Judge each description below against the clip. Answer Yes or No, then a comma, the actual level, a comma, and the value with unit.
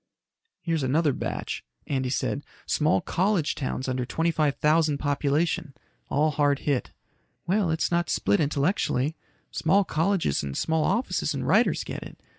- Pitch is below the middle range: No, medium, 150 Hz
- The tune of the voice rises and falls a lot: No, average, 3.0 semitones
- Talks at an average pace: Yes, average, 145 wpm